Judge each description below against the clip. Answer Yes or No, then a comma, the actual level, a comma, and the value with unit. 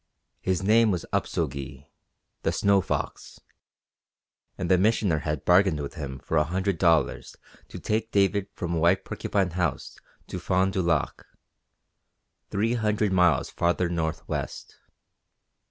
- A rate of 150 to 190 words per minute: No, slow, 135 wpm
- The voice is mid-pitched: No, very low, 90 Hz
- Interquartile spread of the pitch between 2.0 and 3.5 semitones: Yes, average, 3.2 semitones